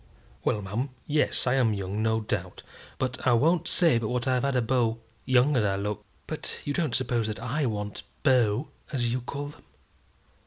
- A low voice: Yes, low, 125 Hz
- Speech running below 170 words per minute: No, average, 195 wpm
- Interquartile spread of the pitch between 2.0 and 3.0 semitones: No, average, 3.7 semitones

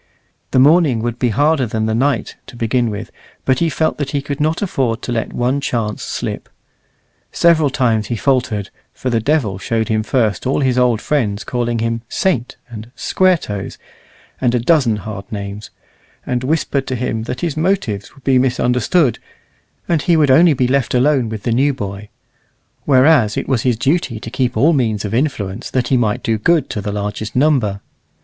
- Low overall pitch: Yes, low, 125 Hz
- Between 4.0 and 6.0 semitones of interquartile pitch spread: Yes, average, 4.3 semitones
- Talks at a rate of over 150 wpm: Yes, average, 190 wpm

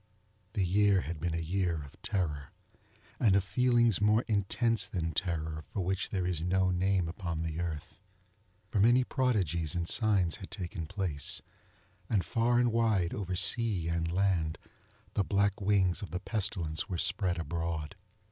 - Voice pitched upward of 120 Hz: No, very low, 95 Hz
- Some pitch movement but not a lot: Yes, average, 3.6 semitones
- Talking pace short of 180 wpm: Yes, average, 160 wpm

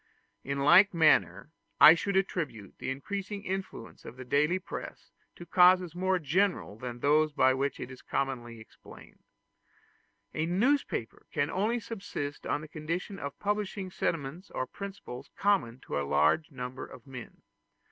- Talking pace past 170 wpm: No, average, 155 wpm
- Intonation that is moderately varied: No, wide, 6.5 semitones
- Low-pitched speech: No, medium, 155 Hz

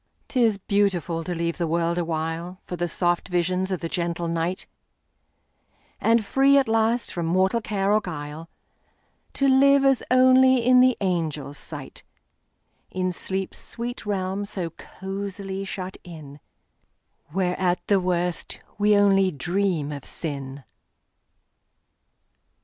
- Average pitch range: Yes, average, 3.5 semitones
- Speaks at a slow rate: Yes, slow, 120 wpm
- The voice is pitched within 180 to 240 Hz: Yes, medium, 185 Hz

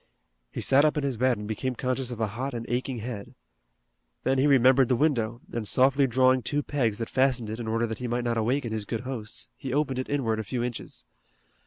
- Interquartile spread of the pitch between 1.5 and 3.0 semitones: Yes, average, 2.7 semitones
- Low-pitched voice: Yes, low, 125 Hz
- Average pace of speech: No, fast, 230 wpm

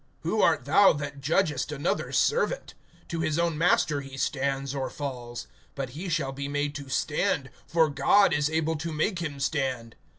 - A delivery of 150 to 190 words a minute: Yes, average, 175 wpm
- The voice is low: No, medium, 145 Hz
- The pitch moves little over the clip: No, average, 3.0 semitones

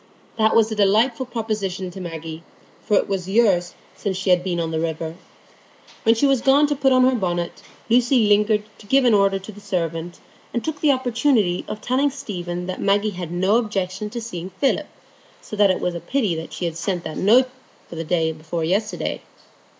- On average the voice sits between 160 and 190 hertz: No, high, 200 Hz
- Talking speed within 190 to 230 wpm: Yes, average, 200 wpm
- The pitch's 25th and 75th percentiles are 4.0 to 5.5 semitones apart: Yes, average, 4.8 semitones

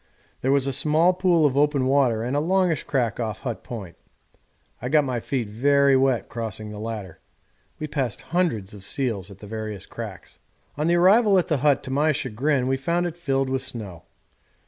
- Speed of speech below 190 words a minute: No, average, 195 wpm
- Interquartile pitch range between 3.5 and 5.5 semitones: Yes, average, 5.2 semitones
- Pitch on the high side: No, low, 135 Hz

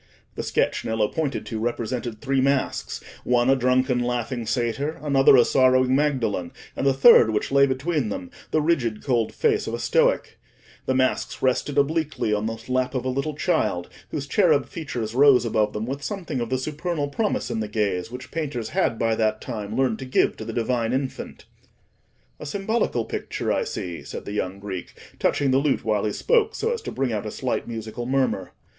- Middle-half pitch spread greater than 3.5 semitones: Yes, average, 4.1 semitones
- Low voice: Yes, low, 130 Hz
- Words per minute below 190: No, average, 195 wpm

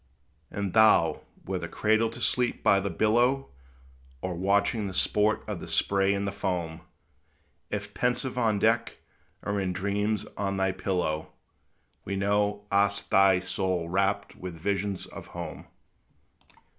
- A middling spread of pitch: No, narrow, 2.0 semitones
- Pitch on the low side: Yes, low, 100 Hz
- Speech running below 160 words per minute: Yes, average, 140 wpm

